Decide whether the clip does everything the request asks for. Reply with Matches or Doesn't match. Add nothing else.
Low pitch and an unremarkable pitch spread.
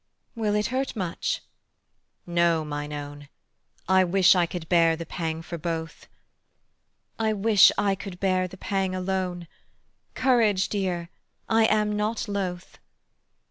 Doesn't match